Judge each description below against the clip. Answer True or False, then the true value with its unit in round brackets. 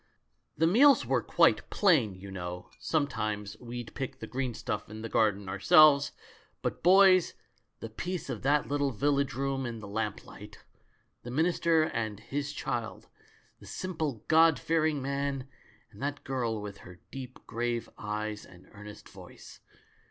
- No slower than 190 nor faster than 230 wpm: False (160 wpm)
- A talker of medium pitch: False (130 Hz)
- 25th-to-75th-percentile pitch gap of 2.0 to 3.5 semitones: False (5.5 semitones)